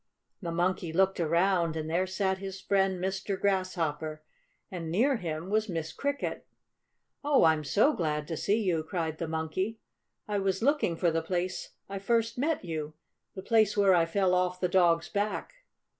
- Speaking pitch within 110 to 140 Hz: No, medium, 185 Hz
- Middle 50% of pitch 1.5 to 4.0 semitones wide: Yes, average, 3.3 semitones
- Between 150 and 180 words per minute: Yes, average, 175 wpm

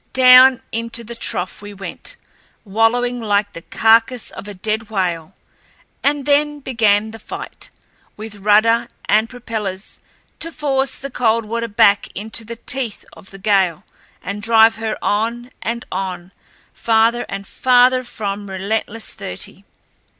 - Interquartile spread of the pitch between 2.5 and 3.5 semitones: Yes, average, 2.9 semitones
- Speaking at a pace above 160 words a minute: No, slow, 135 wpm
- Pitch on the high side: Yes, high, 225 Hz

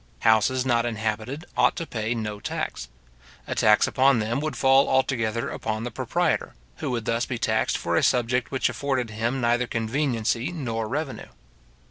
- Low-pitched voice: Yes, low, 120 Hz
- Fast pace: No, average, 165 wpm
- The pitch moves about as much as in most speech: Yes, average, 3.0 semitones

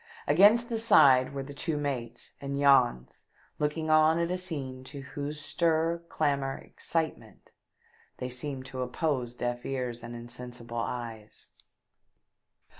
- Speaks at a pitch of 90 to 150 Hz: Yes, medium, 140 Hz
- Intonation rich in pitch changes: No, average, 4.0 semitones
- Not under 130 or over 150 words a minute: Yes, slow, 135 wpm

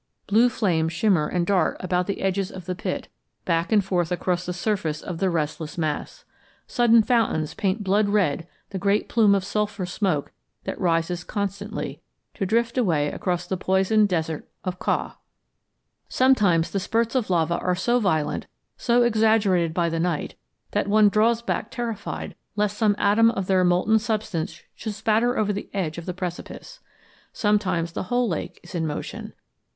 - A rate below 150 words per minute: No, average, 170 wpm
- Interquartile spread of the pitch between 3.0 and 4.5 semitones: Yes, average, 3.7 semitones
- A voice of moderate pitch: No, high, 195 Hz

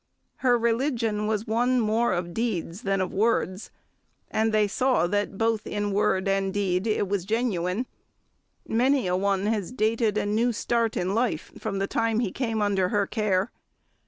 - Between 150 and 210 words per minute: Yes, average, 170 wpm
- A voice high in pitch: Yes, high, 210 Hz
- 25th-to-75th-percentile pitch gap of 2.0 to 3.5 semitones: Yes, average, 2.8 semitones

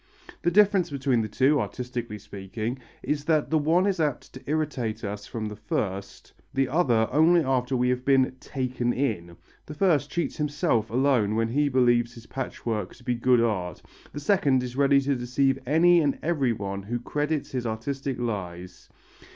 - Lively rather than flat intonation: No, average, 4.4 semitones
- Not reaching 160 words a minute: No, average, 175 wpm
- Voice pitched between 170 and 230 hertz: No, low, 130 Hz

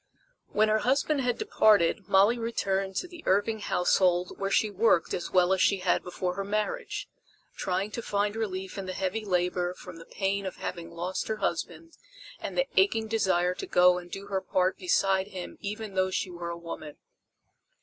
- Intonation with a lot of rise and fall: No, average, 3.0 semitones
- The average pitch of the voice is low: No, high, 195 Hz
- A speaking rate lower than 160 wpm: No, average, 190 wpm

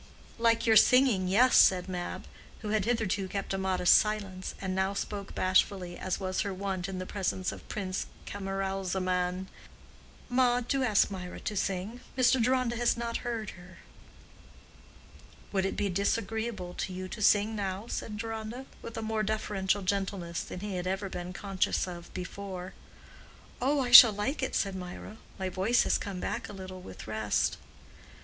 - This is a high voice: Yes, high, 195 Hz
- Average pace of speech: Yes, average, 165 wpm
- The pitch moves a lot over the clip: No, average, 3.0 semitones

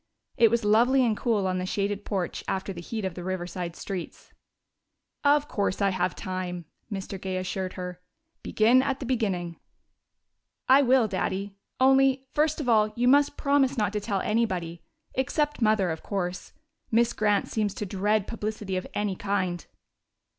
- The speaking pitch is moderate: No, high, 205 Hz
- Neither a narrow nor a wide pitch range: Yes, average, 4.3 semitones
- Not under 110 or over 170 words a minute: Yes, average, 165 wpm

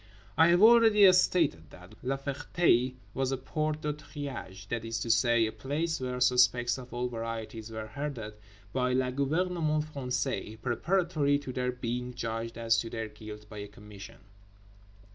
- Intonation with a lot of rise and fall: No, average, 4.6 semitones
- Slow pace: No, average, 160 wpm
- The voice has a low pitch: Yes, low, 125 Hz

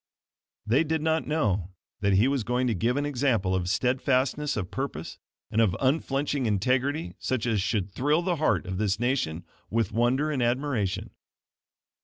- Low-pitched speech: Yes, low, 125 Hz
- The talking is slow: No, average, 165 wpm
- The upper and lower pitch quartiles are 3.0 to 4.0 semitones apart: No, wide, 5.5 semitones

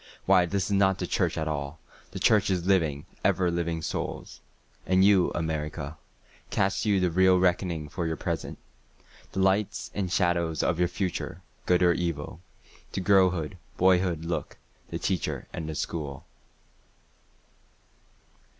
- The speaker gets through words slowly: Yes, slow, 125 wpm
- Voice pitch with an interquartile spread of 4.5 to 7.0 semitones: No, average, 2.8 semitones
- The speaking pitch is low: Yes, very low, 90 Hz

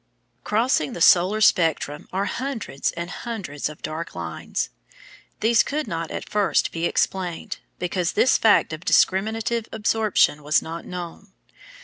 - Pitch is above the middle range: No, medium, 180 Hz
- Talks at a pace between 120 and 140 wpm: Yes, slow, 135 wpm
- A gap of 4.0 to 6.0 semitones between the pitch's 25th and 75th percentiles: Yes, average, 4.9 semitones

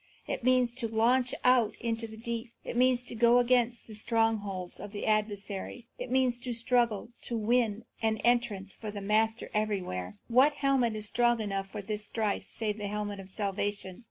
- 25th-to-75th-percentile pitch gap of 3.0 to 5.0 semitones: No, narrow, 2.6 semitones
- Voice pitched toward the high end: Yes, high, 225 Hz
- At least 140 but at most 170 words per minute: No, average, 185 wpm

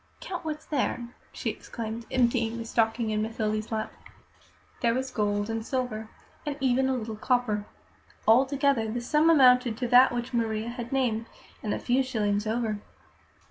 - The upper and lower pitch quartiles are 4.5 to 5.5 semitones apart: No, average, 2.7 semitones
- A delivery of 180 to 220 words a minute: No, average, 160 wpm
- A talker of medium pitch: No, high, 235 Hz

